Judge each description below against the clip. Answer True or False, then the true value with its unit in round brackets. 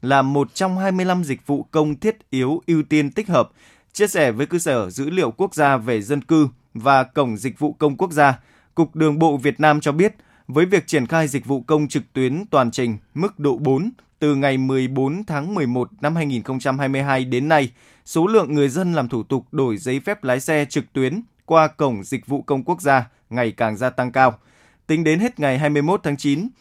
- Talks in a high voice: False (145 Hz)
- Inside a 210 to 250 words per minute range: True (215 wpm)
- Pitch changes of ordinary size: True (3.4 semitones)